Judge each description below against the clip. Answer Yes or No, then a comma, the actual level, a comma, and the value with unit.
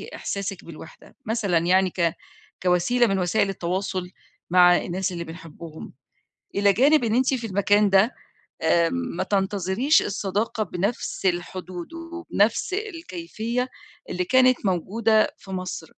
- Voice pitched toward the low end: No, high, 195 Hz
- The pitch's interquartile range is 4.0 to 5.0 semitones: Yes, average, 4.4 semitones